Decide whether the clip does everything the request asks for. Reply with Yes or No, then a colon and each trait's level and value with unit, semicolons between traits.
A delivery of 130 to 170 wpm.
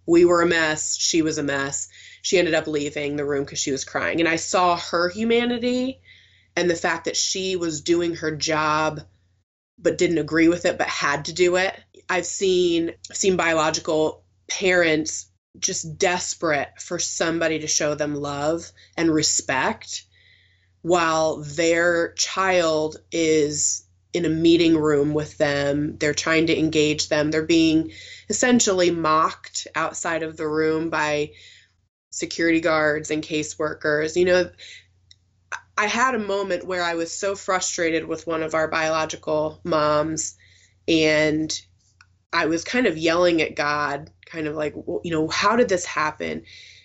Yes: average, 155 wpm